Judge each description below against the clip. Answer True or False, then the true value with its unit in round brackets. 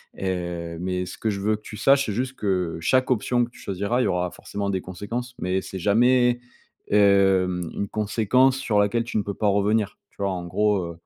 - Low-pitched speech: True (100 Hz)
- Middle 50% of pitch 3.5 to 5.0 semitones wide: True (4.1 semitones)